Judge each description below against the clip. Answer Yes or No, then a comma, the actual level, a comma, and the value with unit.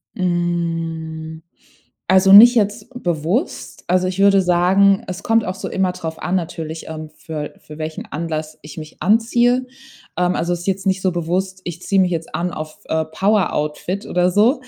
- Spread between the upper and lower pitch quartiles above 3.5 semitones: No, average, 3.2 semitones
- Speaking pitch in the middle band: Yes, medium, 180 Hz